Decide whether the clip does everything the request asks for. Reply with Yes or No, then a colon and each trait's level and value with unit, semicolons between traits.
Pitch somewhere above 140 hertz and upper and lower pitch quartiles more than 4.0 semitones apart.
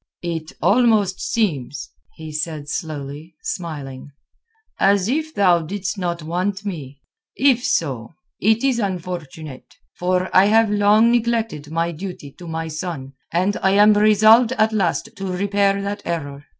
Yes: medium, 185 Hz; average, 4.7 semitones